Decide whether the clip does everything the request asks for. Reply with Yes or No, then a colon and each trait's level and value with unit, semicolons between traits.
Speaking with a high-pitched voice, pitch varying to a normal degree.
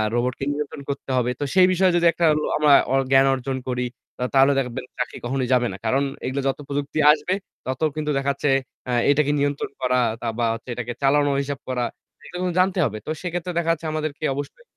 No: medium, 140 Hz; average, 3.4 semitones